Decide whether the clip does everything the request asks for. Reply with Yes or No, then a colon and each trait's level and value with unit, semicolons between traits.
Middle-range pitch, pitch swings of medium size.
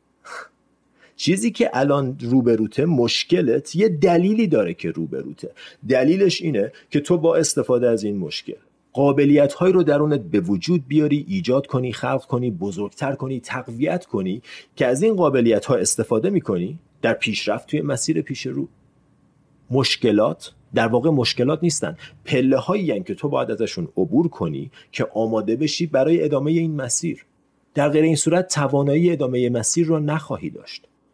Yes: medium, 145 Hz; average, 4.8 semitones